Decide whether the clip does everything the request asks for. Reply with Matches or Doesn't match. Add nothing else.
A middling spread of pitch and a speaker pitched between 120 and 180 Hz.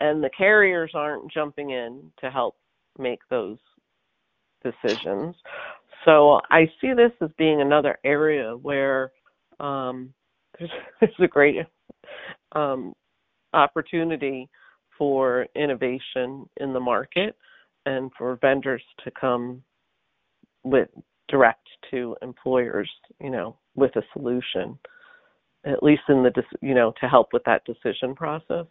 Matches